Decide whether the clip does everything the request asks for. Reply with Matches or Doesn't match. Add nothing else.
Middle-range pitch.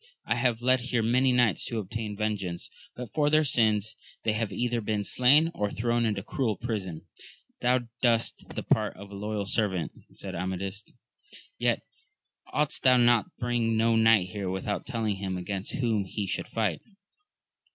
Doesn't match